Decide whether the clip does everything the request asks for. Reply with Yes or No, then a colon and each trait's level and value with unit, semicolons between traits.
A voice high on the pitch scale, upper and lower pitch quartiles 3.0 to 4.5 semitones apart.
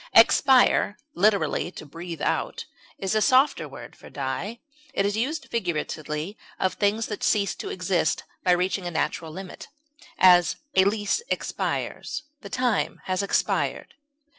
Yes: high, 195 Hz; average, 3.7 semitones